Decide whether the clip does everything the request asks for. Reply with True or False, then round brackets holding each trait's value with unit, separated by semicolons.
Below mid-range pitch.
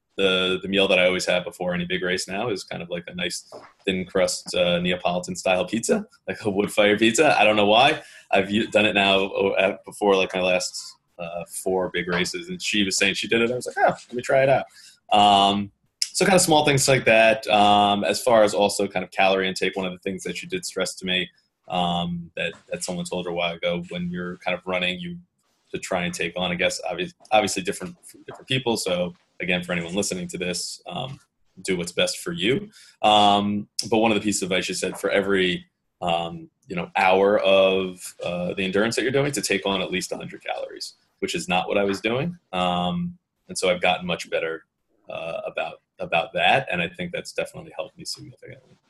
True (95 Hz)